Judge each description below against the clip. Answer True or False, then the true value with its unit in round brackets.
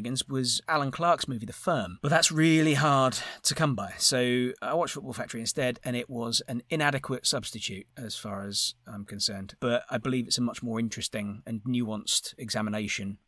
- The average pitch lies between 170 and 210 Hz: False (120 Hz)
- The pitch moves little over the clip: False (3.8 semitones)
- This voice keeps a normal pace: True (185 wpm)